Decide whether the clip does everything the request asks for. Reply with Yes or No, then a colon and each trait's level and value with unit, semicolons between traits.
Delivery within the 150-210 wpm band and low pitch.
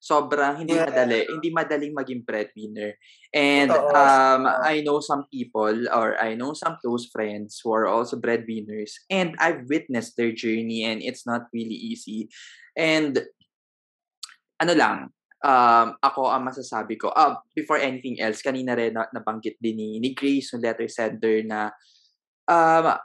Yes: fast, 155 wpm; low, 125 Hz